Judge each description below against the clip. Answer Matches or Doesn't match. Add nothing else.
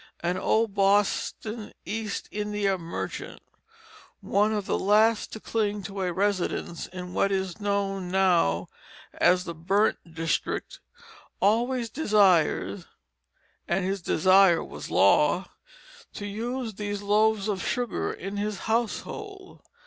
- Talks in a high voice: Matches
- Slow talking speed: Matches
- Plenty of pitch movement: Doesn't match